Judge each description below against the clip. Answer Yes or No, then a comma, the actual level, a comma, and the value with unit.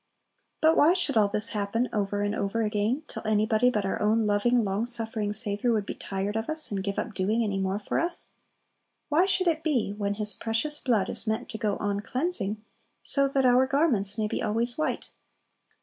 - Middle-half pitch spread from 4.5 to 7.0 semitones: No, average, 3.6 semitones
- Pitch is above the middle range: Yes, high, 220 Hz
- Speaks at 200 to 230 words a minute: Yes, fast, 205 wpm